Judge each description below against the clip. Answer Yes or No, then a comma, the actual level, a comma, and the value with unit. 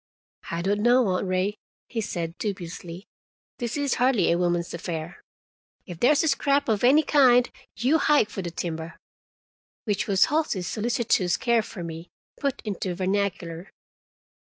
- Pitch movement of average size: No, wide, 5.8 semitones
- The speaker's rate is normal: Yes, average, 150 wpm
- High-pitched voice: Yes, high, 200 Hz